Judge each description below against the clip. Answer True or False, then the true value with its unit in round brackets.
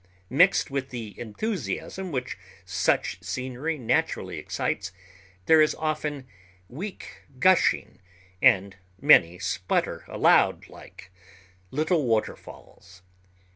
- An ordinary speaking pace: False (95 wpm)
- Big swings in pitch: True (7.5 semitones)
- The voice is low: True (130 Hz)